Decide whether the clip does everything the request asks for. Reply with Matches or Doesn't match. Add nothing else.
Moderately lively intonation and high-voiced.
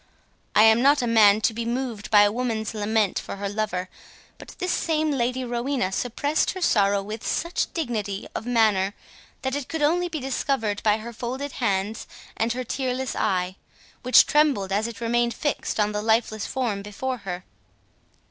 Matches